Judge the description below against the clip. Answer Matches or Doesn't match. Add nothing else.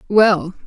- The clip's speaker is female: Matches